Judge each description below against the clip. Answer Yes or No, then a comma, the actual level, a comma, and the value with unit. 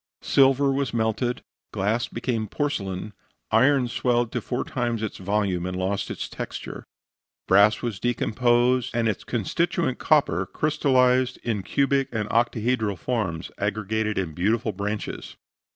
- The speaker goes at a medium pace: No, slow, 130 wpm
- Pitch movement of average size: Yes, average, 3.6 semitones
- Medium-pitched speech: No, low, 115 Hz